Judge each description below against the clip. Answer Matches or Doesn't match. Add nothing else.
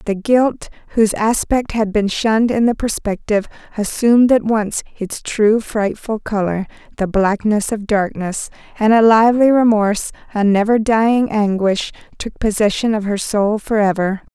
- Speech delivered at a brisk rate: Doesn't match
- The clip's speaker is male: Doesn't match